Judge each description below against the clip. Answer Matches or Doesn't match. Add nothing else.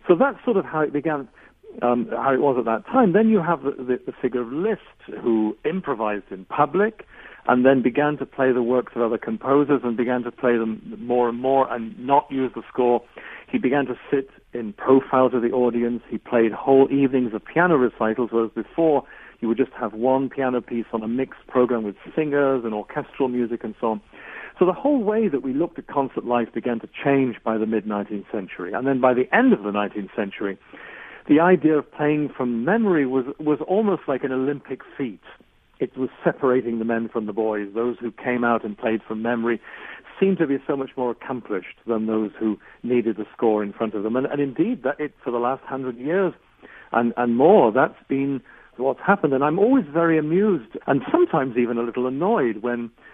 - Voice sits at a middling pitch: Doesn't match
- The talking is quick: Matches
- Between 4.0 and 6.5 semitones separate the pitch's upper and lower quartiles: Doesn't match